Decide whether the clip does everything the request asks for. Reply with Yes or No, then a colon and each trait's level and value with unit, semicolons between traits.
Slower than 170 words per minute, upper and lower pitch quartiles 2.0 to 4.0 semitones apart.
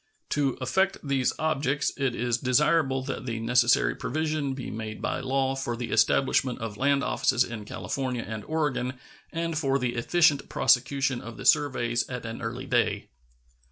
Yes: average, 160 wpm; average, 2.8 semitones